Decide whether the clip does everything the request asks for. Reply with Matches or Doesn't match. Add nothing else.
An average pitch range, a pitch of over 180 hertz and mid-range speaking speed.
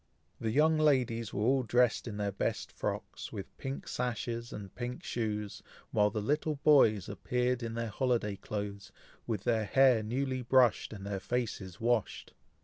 Doesn't match